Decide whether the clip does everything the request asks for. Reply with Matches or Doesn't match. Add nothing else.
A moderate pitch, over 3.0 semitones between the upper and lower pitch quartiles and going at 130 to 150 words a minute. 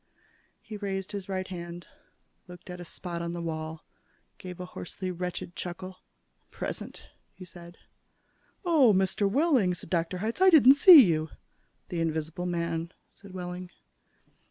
Doesn't match